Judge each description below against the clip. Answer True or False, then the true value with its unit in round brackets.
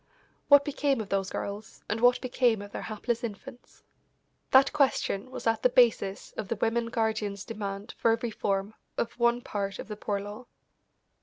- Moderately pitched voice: False (225 Hz)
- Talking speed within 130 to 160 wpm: False (175 wpm)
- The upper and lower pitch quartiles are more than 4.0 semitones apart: False (3.2 semitones)